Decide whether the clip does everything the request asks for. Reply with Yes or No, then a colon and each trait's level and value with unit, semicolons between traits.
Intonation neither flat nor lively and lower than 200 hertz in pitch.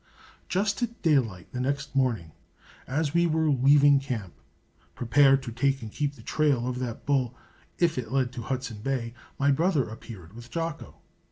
Yes: average, 3.6 semitones; low, 135 Hz